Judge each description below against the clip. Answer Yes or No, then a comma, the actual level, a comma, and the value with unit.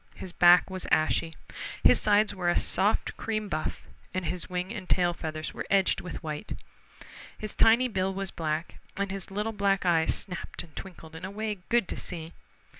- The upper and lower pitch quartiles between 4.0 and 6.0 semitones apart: No, average, 2.9 semitones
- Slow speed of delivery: No, average, 190 wpm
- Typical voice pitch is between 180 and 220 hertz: Yes, medium, 185 Hz